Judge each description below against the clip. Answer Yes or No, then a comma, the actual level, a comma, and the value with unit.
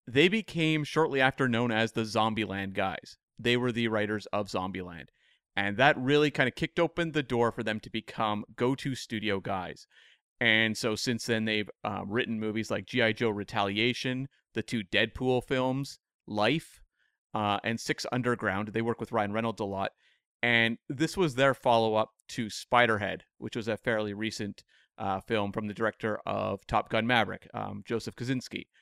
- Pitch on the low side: Yes, low, 115 Hz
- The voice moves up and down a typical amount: Yes, average, 3.0 semitones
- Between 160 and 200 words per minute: Yes, average, 175 wpm